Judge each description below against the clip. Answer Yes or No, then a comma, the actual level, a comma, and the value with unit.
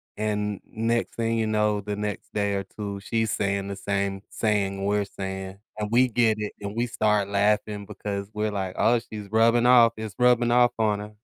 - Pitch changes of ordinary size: No, narrow, 2.1 semitones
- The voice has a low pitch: Yes, low, 105 Hz